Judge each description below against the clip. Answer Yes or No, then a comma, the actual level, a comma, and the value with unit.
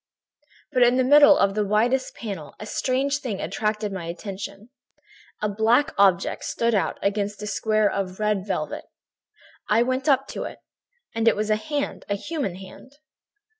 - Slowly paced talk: No, average, 165 wpm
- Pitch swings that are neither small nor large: Yes, average, 4.3 semitones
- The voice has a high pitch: Yes, high, 215 Hz